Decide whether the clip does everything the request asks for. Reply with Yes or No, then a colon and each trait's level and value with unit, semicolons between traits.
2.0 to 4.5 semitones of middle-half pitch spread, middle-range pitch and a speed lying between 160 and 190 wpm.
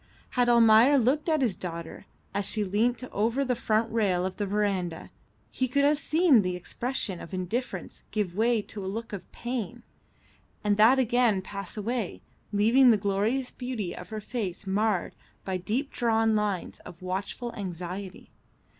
No: average, 4.1 semitones; high, 215 Hz; average, 165 wpm